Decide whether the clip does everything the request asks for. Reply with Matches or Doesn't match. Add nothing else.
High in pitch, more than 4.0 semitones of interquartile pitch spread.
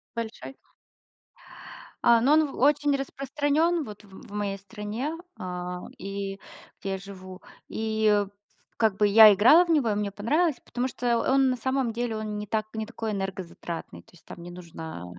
Matches